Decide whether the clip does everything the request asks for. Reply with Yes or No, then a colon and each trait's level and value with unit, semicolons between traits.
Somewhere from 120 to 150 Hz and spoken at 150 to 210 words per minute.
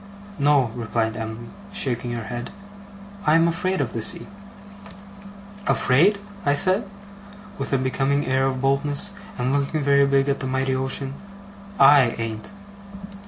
No: low, 135 Hz; slow, 135 wpm